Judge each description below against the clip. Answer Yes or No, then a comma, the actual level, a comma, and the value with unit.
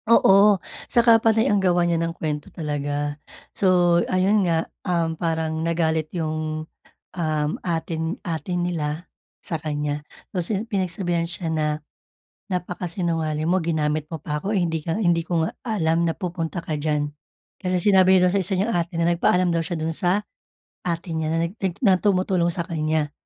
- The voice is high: No, medium, 170 Hz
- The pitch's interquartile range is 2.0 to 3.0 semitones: Yes, narrow, 2.5 semitones